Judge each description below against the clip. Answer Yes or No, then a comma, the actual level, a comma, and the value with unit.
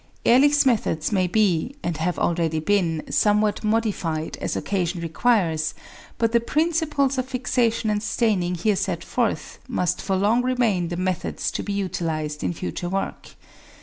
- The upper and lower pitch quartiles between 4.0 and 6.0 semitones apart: Yes, average, 5.3 semitones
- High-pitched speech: Yes, high, 200 Hz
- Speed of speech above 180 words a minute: No, average, 150 wpm